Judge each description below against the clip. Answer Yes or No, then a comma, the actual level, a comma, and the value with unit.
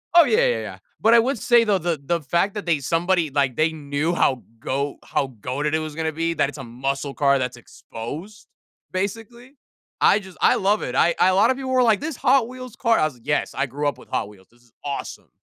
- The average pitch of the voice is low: No, medium, 165 Hz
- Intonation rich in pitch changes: Yes, wide, 7.8 semitones